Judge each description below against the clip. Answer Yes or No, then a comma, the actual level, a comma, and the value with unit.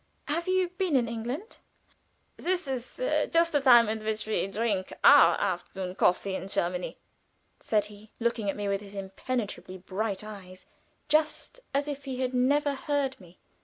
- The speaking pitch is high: Yes, high, 230 Hz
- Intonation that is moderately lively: No, wide, 6.2 semitones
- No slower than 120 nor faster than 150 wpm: No, average, 165 wpm